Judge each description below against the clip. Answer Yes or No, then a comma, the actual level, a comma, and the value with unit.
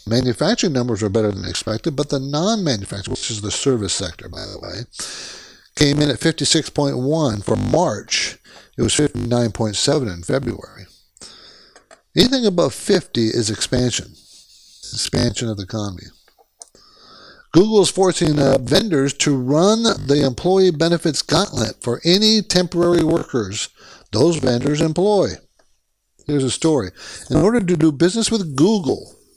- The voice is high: No, medium, 140 Hz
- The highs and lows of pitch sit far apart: Yes, wide, 7.1 semitones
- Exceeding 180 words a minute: No, slow, 135 wpm